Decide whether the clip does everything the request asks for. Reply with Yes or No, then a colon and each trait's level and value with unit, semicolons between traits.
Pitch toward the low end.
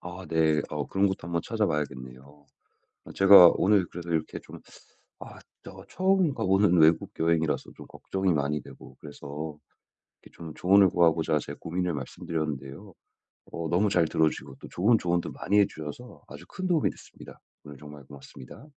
Yes: very low, 85 Hz